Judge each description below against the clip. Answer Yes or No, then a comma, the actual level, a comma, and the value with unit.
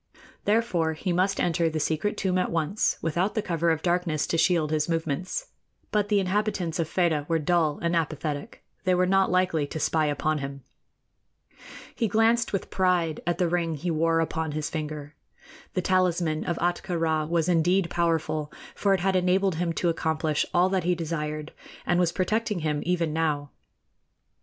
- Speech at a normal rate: Yes, average, 175 wpm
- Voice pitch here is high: No, medium, 170 Hz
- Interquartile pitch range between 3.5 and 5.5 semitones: No, average, 2.7 semitones